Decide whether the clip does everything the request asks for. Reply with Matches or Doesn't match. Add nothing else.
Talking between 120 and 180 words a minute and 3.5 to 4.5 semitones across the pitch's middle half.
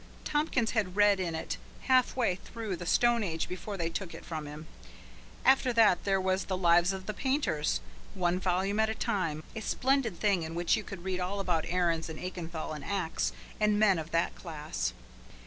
Doesn't match